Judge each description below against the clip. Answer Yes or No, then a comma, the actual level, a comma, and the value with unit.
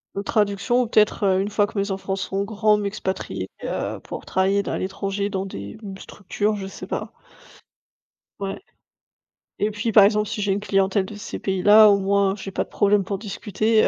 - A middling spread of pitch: No, narrow, 1.4 semitones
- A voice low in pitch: No, high, 200 Hz